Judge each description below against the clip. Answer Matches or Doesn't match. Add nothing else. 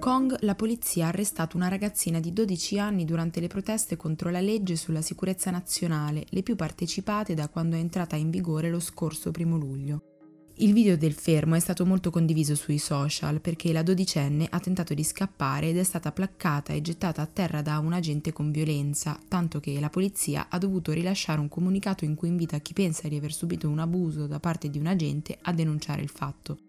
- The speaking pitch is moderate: Matches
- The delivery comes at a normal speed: Doesn't match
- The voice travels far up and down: Doesn't match